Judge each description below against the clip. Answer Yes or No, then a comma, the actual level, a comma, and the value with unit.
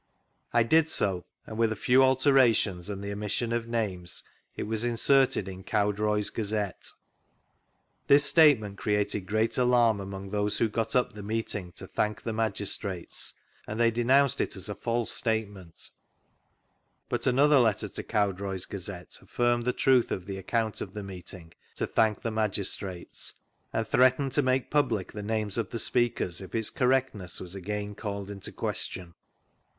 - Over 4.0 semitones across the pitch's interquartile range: No, average, 3.3 semitones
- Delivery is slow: No, average, 165 wpm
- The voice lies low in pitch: Yes, low, 110 Hz